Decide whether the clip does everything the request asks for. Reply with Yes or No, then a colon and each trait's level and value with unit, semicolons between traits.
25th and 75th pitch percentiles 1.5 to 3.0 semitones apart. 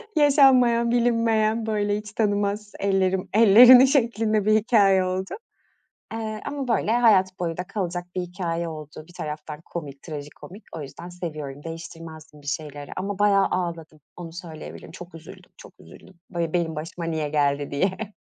No: average, 4.9 semitones